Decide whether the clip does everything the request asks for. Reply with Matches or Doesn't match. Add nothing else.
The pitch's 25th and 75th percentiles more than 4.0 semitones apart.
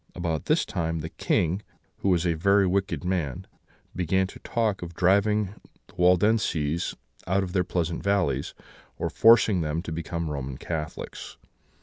Doesn't match